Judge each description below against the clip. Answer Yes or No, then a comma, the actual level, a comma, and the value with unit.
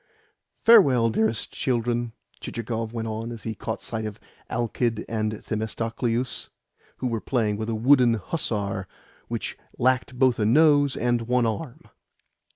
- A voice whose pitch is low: Yes, low, 115 Hz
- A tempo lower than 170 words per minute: Yes, average, 140 wpm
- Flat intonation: Yes, narrow, 2.1 semitones